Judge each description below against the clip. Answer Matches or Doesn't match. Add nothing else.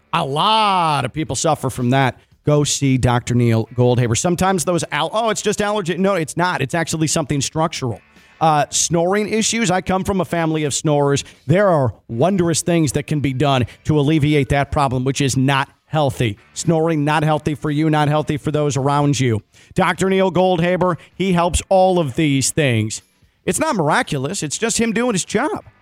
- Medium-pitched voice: Matches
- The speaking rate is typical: Matches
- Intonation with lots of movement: Doesn't match